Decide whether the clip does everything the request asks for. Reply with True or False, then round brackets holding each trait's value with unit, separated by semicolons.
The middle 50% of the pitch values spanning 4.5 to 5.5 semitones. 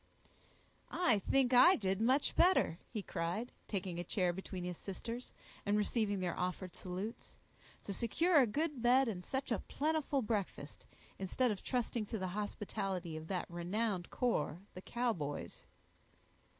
True (5.2 semitones)